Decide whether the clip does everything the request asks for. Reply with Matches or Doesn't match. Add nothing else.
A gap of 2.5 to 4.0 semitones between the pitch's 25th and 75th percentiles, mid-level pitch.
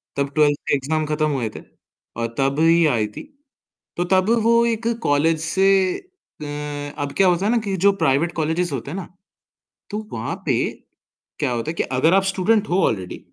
Doesn't match